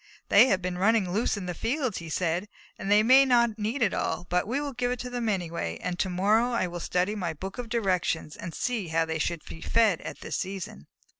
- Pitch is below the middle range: No, high, 195 Hz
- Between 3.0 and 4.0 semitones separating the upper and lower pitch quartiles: No, average, 4.8 semitones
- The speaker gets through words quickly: Yes, fast, 240 wpm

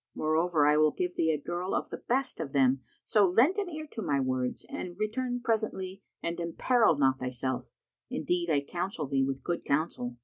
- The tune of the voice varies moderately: No, wide, 7.1 semitones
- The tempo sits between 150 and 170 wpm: No, average, 195 wpm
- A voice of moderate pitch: Yes, medium, 170 Hz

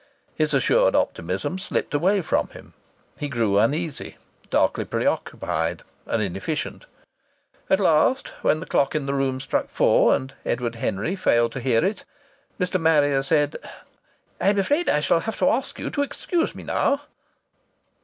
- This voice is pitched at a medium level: Yes, medium, 150 Hz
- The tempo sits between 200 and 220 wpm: No, average, 155 wpm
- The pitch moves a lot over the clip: Yes, wide, 7.4 semitones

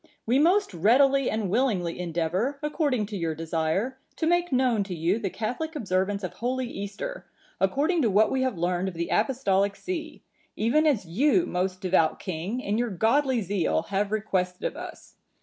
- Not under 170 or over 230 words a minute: Yes, average, 180 wpm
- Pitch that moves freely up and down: Yes, wide, 6.2 semitones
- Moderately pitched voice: No, high, 210 Hz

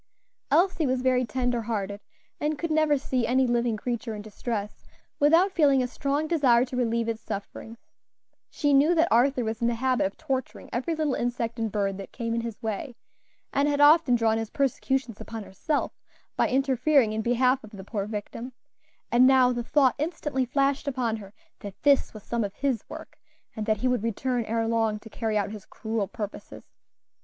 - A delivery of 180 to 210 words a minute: Yes, average, 190 wpm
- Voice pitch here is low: No, high, 245 Hz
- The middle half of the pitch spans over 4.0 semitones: No, average, 3.7 semitones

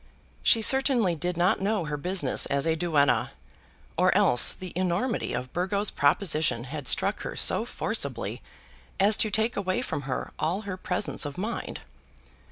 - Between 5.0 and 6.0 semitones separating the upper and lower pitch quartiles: Yes, wide, 5.4 semitones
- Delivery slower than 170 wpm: Yes, average, 160 wpm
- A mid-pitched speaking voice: Yes, medium, 180 Hz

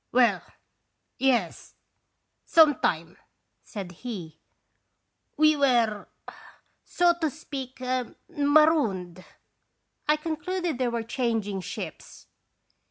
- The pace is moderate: No, slow, 90 wpm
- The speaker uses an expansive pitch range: Yes, wide, 6.9 semitones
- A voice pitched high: Yes, very high, 250 Hz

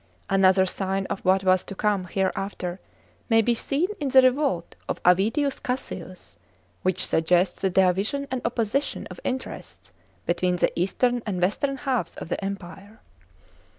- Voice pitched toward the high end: Yes, high, 195 Hz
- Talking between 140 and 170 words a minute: Yes, average, 155 wpm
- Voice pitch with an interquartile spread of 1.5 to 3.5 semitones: No, average, 5.2 semitones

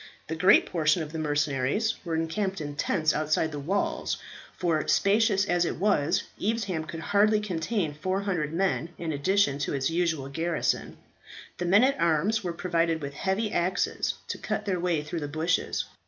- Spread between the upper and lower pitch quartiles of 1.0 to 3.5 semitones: No, average, 3.9 semitones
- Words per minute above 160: Yes, average, 170 wpm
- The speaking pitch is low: No, medium, 170 Hz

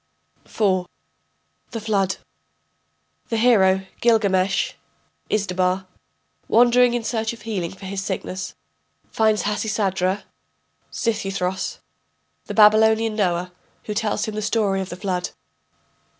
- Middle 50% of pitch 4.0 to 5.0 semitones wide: No, narrow, 2.6 semitones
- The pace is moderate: No, slow, 110 wpm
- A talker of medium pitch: No, high, 205 Hz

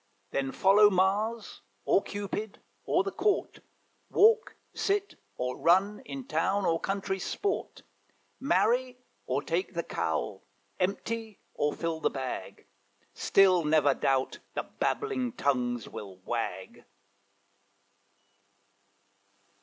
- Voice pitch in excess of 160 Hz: Yes, high, 190 Hz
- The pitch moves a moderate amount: No, wide, 8.3 semitones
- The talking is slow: Yes, slow, 105 wpm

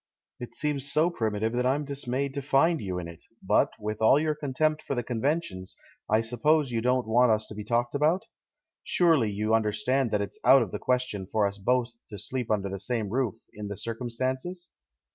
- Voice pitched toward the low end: Yes, low, 120 Hz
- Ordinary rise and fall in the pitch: Yes, average, 4.5 semitones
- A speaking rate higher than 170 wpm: Yes, average, 200 wpm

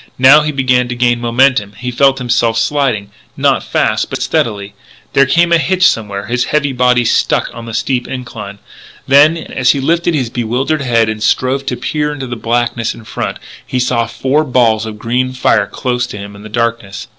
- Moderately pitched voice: No, low, 125 Hz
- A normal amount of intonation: Yes, average, 3.0 semitones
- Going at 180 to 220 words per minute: Yes, average, 190 wpm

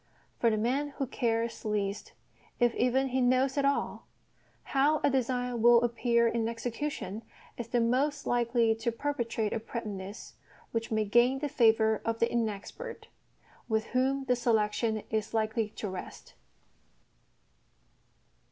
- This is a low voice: No, high, 235 Hz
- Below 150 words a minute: Yes, average, 140 wpm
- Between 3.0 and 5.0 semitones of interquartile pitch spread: No, narrow, 2.6 semitones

